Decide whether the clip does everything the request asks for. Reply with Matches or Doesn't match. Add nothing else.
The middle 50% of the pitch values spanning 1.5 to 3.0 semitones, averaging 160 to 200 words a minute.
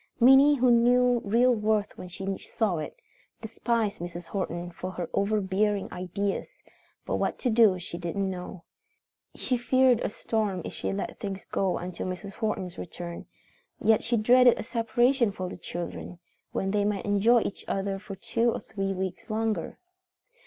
Doesn't match